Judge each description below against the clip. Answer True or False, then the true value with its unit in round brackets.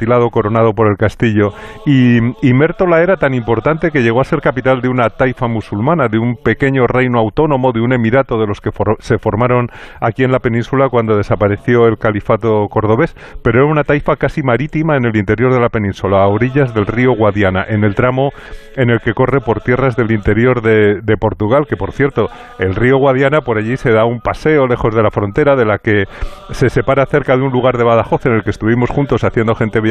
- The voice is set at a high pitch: False (120 Hz)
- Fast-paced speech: True (215 wpm)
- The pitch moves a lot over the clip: False (3.2 semitones)